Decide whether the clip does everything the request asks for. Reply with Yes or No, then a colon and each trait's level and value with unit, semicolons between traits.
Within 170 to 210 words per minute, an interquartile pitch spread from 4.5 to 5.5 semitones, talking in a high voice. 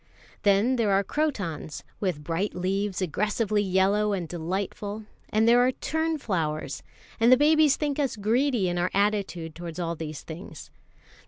No: average, 150 wpm; average, 4.8 semitones; high, 200 Hz